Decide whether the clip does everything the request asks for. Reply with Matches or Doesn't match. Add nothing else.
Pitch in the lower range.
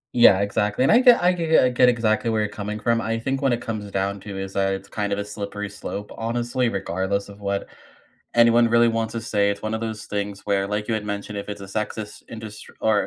Matches